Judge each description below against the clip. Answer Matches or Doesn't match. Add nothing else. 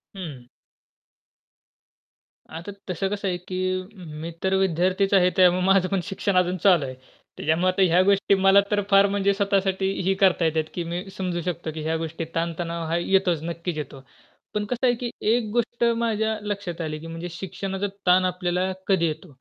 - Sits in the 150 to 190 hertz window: Matches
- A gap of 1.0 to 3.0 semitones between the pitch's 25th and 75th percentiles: Matches